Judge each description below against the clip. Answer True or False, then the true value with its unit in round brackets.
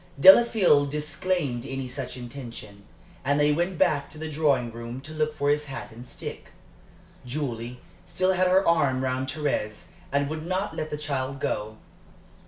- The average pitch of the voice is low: False (145 Hz)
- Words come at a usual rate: True (165 wpm)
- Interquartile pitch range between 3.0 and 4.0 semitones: True (3.7 semitones)